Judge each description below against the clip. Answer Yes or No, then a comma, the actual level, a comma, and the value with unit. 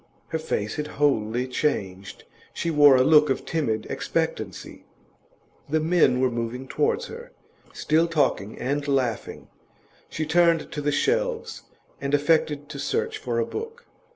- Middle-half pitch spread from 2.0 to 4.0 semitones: No, average, 4.4 semitones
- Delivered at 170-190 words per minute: No, average, 145 wpm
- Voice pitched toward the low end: No, medium, 145 Hz